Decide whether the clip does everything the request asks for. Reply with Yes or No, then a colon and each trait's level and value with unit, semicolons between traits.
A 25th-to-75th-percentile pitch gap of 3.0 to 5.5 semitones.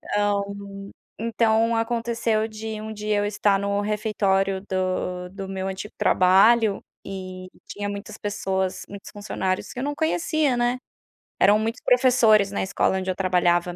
No: narrow, 2.6 semitones